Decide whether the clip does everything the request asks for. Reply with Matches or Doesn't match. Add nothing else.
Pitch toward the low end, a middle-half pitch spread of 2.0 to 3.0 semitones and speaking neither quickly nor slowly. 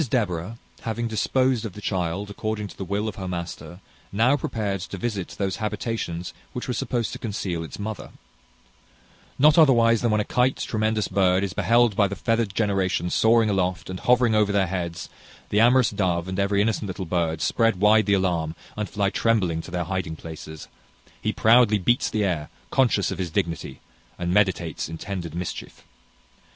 Doesn't match